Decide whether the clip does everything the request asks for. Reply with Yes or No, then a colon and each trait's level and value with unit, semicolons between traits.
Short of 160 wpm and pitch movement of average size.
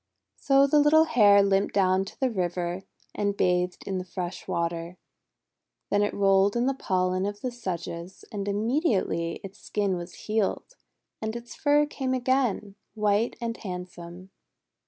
Yes: average, 150 wpm; average, 4.6 semitones